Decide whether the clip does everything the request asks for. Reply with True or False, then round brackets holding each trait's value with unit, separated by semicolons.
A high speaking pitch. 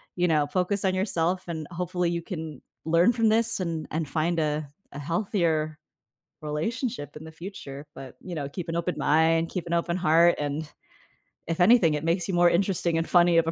False (170 Hz)